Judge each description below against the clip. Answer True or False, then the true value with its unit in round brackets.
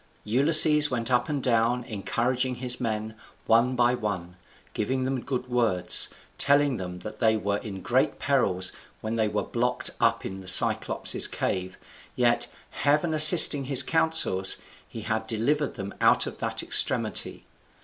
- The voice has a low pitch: True (120 Hz)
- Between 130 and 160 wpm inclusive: True (150 wpm)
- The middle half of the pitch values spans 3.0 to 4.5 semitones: True (3.9 semitones)